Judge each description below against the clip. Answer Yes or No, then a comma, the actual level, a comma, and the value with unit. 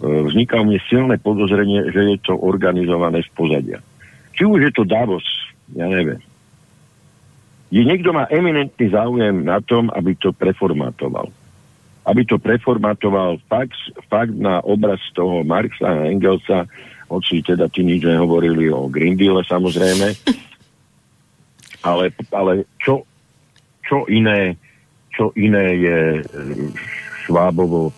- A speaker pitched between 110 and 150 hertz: No, low, 100 Hz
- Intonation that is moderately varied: Yes, average, 4.8 semitones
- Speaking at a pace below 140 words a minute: Yes, average, 120 wpm